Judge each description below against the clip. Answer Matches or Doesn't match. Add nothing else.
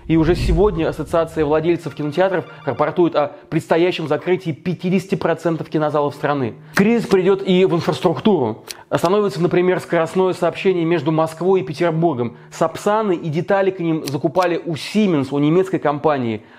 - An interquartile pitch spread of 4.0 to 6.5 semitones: Doesn't match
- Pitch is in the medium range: Matches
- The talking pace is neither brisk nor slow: Matches